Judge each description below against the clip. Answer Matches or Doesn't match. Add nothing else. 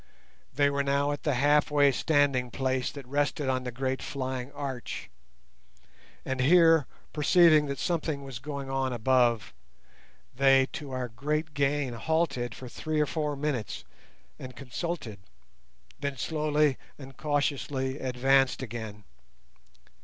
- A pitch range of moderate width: Doesn't match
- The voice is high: Doesn't match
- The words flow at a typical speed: Doesn't match